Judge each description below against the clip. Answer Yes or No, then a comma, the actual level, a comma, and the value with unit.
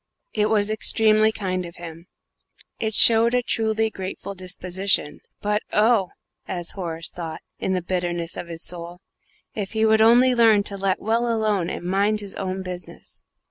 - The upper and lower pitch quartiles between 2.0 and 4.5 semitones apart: Yes, average, 3.5 semitones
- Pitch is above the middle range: Yes, high, 195 Hz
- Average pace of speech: Yes, average, 165 wpm